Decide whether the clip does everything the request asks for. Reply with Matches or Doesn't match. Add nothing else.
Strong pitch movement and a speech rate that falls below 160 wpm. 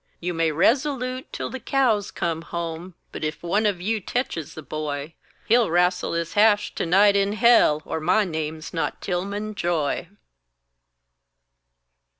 Doesn't match